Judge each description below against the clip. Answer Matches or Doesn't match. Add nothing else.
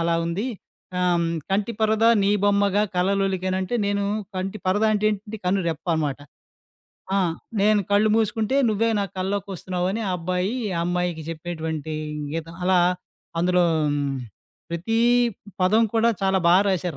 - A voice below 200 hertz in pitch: Matches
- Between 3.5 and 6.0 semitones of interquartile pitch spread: Doesn't match